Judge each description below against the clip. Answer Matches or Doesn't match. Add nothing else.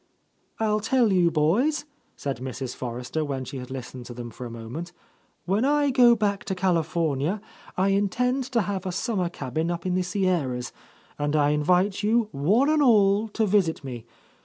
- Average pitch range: Doesn't match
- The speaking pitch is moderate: Matches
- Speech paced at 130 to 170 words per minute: Doesn't match